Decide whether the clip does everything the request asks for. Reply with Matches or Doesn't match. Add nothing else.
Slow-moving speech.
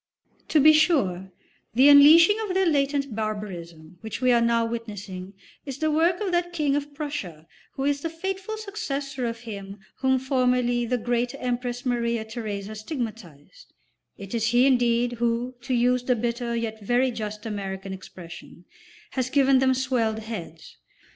Doesn't match